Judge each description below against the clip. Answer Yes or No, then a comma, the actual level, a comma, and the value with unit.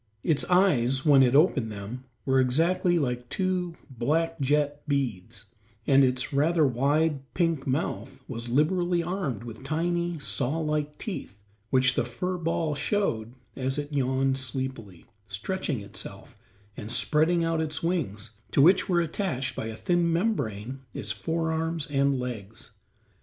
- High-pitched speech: No, medium, 140 Hz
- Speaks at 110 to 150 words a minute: Yes, average, 140 wpm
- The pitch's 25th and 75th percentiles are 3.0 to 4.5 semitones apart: No, average, 5.0 semitones